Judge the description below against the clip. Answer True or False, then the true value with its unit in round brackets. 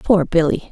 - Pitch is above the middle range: False (175 Hz)